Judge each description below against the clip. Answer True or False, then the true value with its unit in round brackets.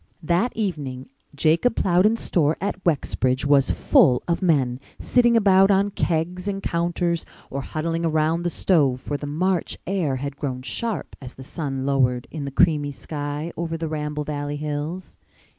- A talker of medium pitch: True (155 Hz)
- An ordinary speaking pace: True (160 wpm)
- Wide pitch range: False (3.9 semitones)